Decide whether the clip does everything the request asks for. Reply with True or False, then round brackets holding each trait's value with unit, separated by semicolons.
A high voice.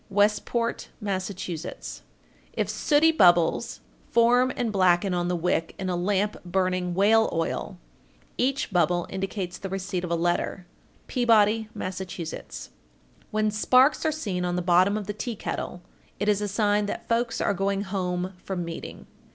True (195 Hz)